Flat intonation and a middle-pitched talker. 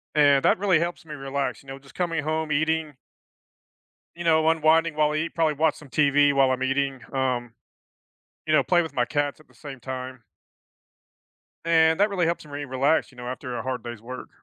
No: average, 3.3 semitones; medium, 145 Hz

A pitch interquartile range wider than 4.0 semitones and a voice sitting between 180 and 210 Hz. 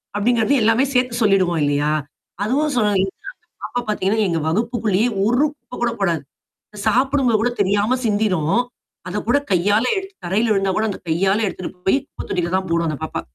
Yes: average, 4.4 semitones; high, 205 Hz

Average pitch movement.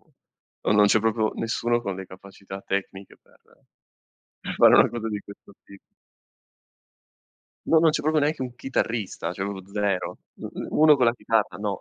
Yes: average, 3.4 semitones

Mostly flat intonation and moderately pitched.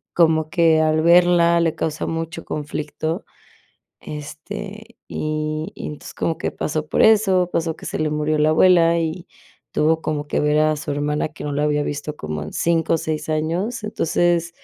Yes: narrow, 2.0 semitones; medium, 160 Hz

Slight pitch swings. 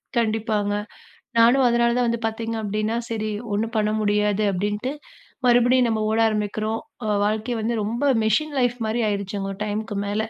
Yes: narrow, 2.1 semitones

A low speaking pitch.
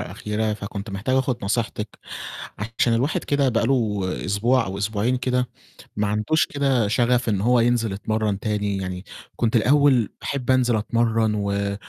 Yes: low, 115 Hz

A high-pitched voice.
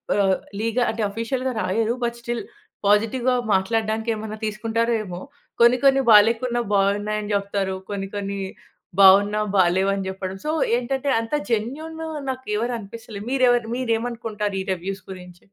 Yes: high, 215 Hz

